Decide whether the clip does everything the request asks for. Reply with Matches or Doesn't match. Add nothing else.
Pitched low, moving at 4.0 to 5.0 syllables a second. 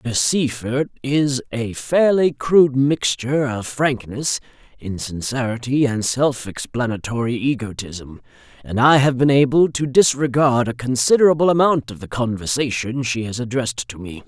Matches